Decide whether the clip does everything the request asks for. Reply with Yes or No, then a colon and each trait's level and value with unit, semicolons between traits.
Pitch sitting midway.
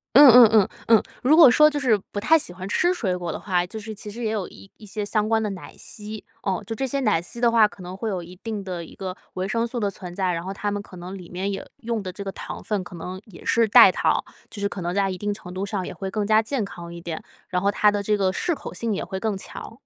No: high, 205 Hz